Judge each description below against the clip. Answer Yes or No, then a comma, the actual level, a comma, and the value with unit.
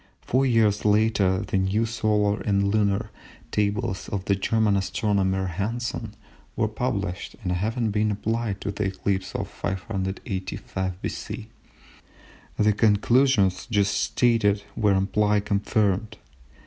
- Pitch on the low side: Yes, low, 105 Hz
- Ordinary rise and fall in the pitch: No, narrow, 2.0 semitones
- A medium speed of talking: No, slow, 120 wpm